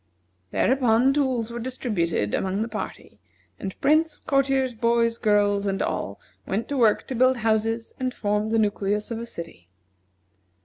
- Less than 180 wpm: Yes, average, 150 wpm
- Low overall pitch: No, high, 225 Hz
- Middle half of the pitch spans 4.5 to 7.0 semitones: No, average, 3.7 semitones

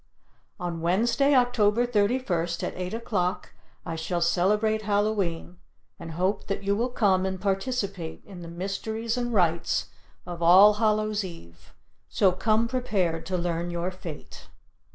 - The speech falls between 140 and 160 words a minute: Yes, average, 145 wpm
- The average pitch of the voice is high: Yes, high, 195 Hz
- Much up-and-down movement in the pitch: No, average, 3.8 semitones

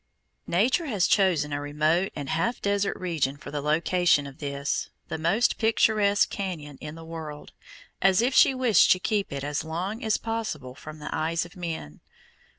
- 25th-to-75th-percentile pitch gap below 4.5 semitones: No, wide, 5.4 semitones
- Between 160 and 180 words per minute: Yes, average, 175 wpm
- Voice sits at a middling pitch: Yes, medium, 170 Hz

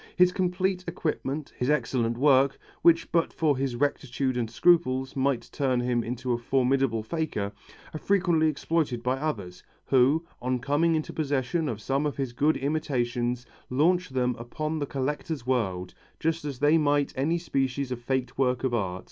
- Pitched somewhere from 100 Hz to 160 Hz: Yes, low, 135 Hz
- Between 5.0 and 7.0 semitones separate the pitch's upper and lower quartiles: No, average, 3.9 semitones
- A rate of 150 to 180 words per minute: Yes, average, 165 wpm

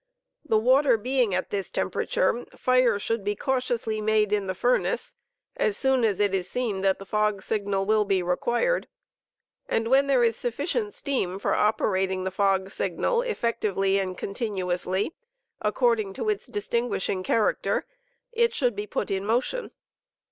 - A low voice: No, high, 215 Hz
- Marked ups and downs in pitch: No, average, 4.6 semitones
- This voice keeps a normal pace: Yes, average, 155 wpm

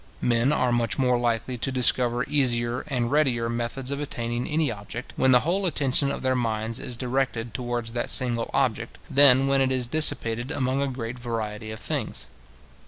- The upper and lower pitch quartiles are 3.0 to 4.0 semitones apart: No, narrow, 2.4 semitones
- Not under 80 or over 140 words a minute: No, average, 180 wpm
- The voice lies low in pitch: Yes, low, 125 Hz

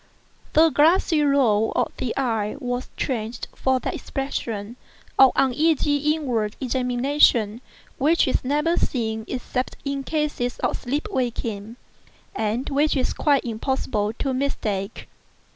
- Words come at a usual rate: No, slow, 125 wpm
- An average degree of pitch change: Yes, average, 4.0 semitones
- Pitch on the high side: Yes, very high, 260 Hz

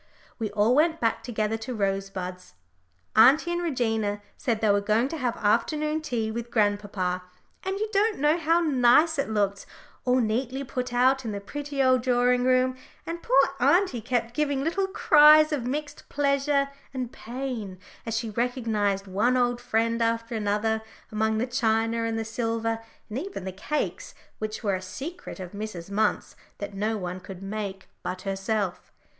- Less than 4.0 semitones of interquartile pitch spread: No, average, 4.5 semitones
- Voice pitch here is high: Yes, high, 230 Hz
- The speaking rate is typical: Yes, average, 170 wpm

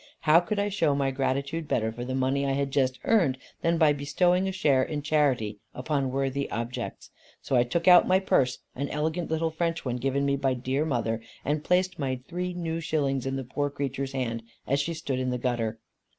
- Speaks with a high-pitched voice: No, medium, 140 Hz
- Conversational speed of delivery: No, fast, 210 wpm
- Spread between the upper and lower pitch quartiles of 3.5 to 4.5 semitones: Yes, average, 3.8 semitones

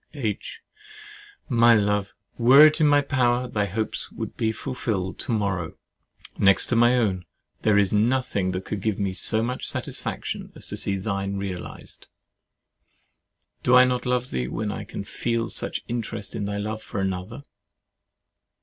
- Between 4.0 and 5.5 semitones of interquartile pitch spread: No, average, 3.6 semitones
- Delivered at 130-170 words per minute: Yes, average, 165 wpm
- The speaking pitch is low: Yes, low, 110 Hz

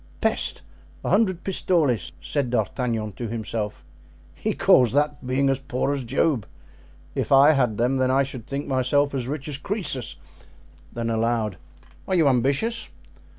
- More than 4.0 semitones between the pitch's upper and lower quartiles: No, average, 3.4 semitones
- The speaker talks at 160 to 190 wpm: No, average, 150 wpm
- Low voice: Yes, low, 130 Hz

